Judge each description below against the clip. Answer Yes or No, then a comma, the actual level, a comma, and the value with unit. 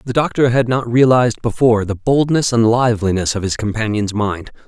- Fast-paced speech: No, average, 180 wpm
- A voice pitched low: Yes, low, 115 Hz